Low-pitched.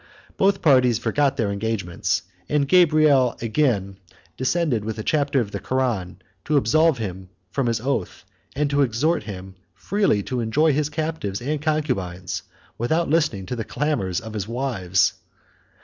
Yes: low, 125 Hz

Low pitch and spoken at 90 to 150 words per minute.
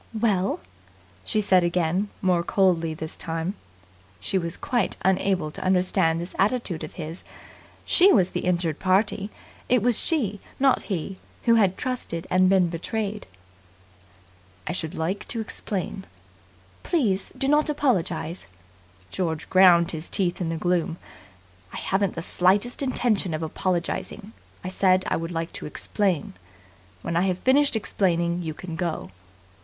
No: medium, 185 Hz; average, 145 wpm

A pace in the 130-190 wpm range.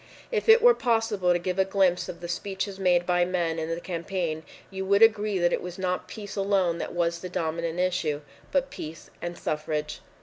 No: fast, 205 wpm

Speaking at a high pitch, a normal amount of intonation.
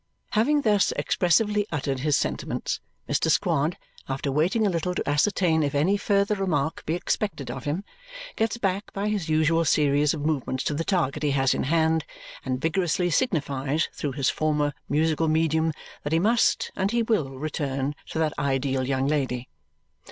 No: medium, 155 Hz; average, 4.9 semitones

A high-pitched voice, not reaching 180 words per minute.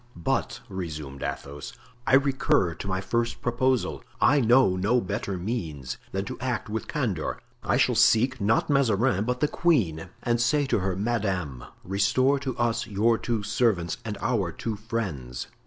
No: low, 110 Hz; average, 160 wpm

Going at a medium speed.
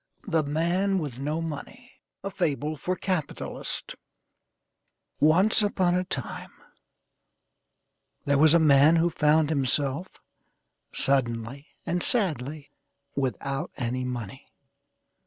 No: slow, 100 wpm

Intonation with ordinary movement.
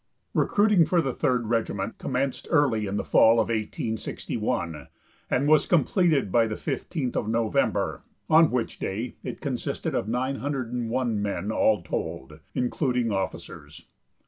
Yes: average, 4.3 semitones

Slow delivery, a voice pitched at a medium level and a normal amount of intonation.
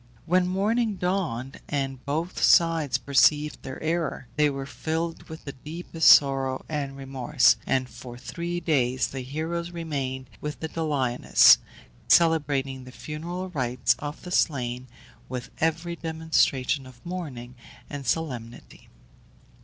Yes: slow, 130 wpm; medium, 145 Hz; average, 4.0 semitones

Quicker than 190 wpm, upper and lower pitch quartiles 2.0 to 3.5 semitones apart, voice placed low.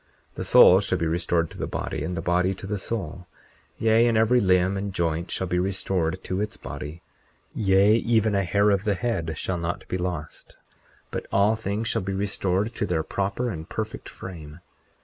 Yes: average, 200 wpm; average, 3.0 semitones; very low, 95 Hz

